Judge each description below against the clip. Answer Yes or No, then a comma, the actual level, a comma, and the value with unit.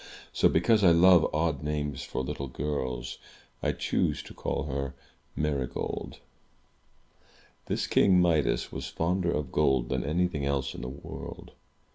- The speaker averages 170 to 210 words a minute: No, average, 140 wpm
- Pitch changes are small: No, average, 3.8 semitones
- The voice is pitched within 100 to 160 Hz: No, very low, 75 Hz